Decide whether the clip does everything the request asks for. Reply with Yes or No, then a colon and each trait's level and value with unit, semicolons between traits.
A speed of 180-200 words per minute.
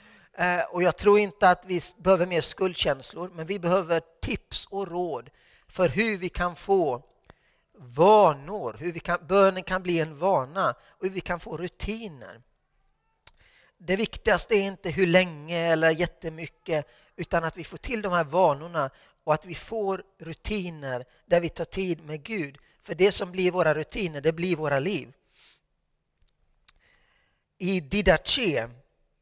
No: average, 150 wpm